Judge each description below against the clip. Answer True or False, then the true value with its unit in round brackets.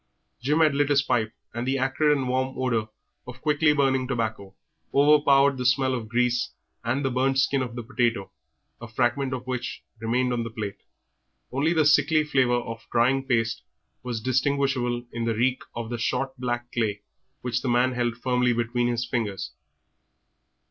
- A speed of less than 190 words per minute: True (175 wpm)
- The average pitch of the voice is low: True (125 Hz)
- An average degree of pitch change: False (2.2 semitones)